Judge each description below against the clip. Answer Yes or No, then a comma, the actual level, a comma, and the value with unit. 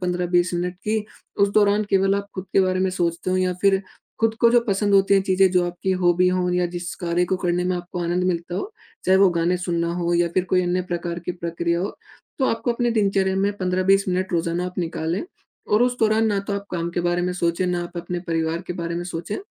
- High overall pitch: No, medium, 180 Hz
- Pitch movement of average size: No, narrow, 1.9 semitones